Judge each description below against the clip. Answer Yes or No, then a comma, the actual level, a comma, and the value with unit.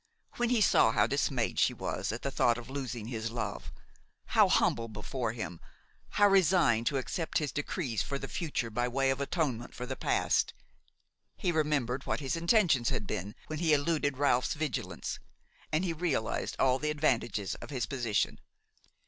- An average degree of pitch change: Yes, average, 4.8 semitones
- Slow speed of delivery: No, average, 165 wpm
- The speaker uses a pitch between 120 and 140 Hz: Yes, low, 135 Hz